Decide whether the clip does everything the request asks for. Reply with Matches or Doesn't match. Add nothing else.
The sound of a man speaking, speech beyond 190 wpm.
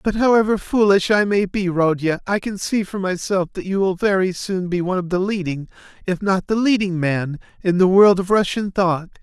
Matches